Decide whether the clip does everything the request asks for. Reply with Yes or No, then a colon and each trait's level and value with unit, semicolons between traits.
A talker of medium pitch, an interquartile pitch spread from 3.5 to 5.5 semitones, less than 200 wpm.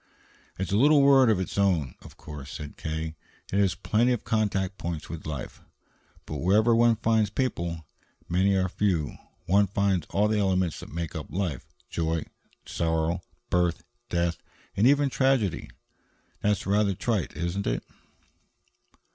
No: very low, 95 Hz; average, 4.2 semitones; average, 160 wpm